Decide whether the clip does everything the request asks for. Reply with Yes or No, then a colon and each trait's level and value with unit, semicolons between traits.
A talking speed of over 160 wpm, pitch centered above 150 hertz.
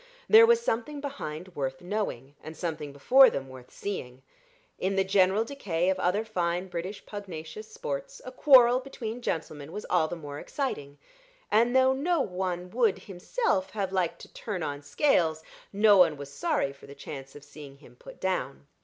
Yes: average, 175 wpm; medium, 185 Hz